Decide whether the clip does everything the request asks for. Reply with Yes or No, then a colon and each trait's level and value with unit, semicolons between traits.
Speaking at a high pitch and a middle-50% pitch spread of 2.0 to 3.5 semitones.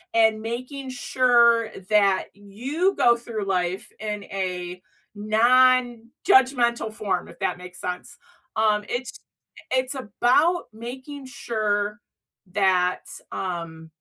No: high, 220 Hz; average, 4.4 semitones